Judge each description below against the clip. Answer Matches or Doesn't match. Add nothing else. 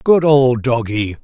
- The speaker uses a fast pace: Doesn't match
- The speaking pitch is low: Matches